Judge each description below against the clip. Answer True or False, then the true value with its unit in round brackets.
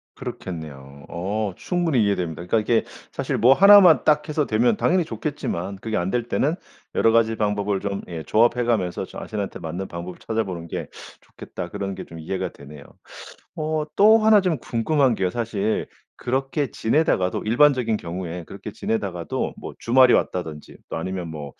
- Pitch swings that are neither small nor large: False (6.8 semitones)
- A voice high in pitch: False (110 Hz)